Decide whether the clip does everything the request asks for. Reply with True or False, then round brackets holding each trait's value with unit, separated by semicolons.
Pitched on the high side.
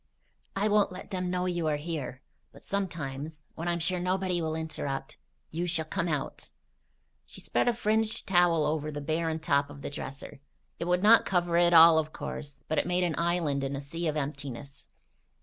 False (165 Hz)